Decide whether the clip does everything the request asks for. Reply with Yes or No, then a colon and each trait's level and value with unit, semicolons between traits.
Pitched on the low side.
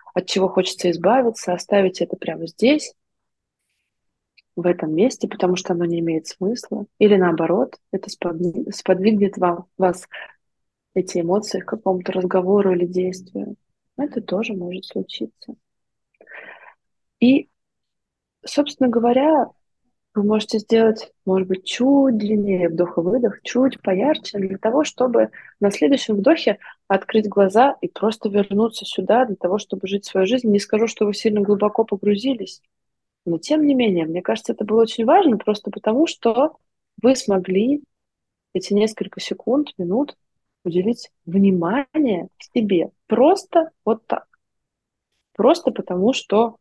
No: high, 205 Hz